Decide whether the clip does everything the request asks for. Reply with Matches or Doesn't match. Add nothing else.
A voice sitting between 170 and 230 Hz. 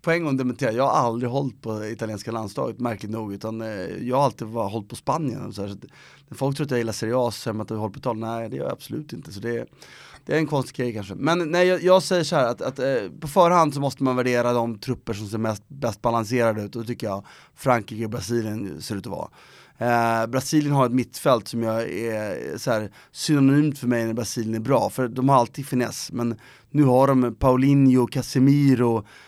Doesn't match